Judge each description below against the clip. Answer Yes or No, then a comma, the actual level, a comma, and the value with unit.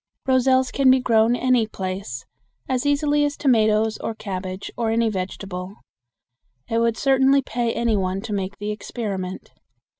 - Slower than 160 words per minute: Yes, average, 150 wpm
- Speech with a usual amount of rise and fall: Yes, average, 4.6 semitones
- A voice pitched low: No, high, 225 Hz